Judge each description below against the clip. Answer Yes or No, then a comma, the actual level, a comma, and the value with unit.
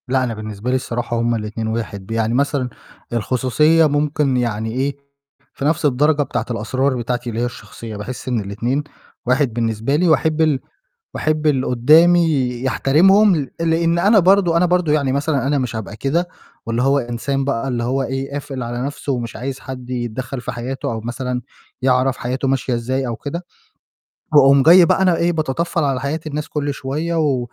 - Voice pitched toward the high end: No, low, 135 Hz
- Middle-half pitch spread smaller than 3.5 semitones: No, average, 4.0 semitones